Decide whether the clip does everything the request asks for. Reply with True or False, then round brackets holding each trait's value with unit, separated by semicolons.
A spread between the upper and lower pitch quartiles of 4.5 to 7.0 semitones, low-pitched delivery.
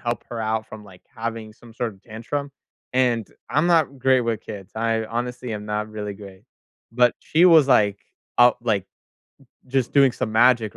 False (2.7 semitones; 115 Hz)